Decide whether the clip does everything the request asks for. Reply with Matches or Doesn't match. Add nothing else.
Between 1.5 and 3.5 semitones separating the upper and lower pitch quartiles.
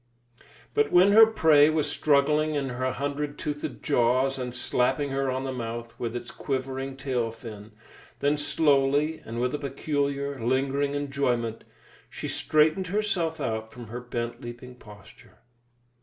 Matches